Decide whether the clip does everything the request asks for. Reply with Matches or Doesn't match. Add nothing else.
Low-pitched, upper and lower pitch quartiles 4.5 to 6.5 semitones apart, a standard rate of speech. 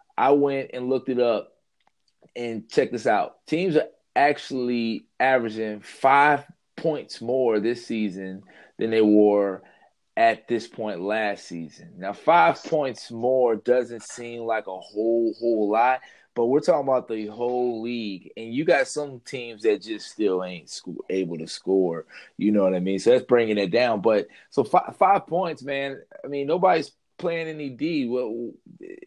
Matches